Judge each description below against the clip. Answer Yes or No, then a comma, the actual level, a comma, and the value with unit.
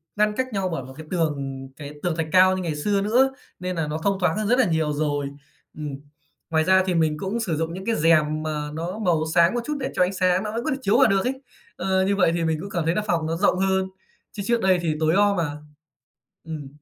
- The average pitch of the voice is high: No, medium, 180 Hz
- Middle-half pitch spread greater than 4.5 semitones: No, average, 4.1 semitones